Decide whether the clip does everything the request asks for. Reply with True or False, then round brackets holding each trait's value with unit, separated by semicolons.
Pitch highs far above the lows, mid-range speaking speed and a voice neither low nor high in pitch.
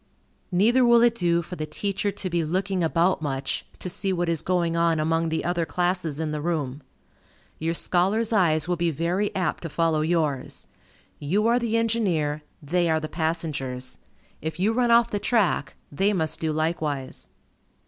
False (3.7 semitones; 180 wpm; 170 Hz)